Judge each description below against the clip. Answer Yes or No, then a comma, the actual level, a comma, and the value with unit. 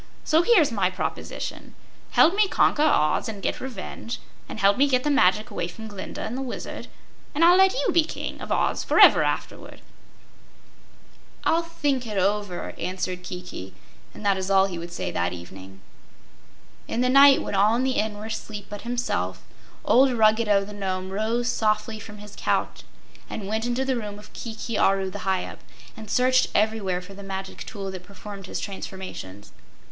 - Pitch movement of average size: Yes, average, 4.4 semitones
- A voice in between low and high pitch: No, high, 210 Hz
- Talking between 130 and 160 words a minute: No, average, 180 wpm